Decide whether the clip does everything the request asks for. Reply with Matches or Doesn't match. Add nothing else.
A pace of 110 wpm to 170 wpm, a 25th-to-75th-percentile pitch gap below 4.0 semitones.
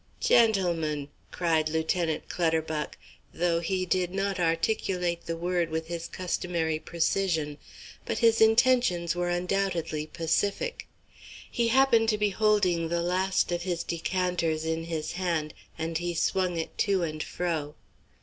Matches